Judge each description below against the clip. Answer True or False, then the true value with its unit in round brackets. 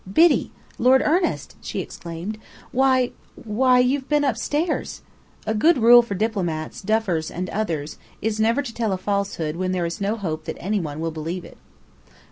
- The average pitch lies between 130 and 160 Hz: False (215 Hz)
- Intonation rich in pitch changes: True (6.3 semitones)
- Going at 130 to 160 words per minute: False (175 wpm)